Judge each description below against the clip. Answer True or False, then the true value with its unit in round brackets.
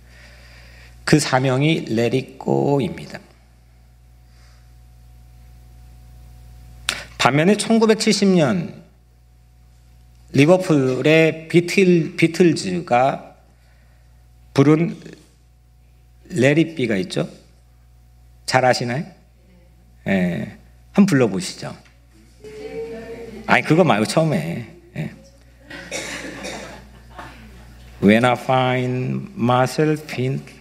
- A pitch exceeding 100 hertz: False (65 Hz)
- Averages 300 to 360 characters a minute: False (140 characters per minute)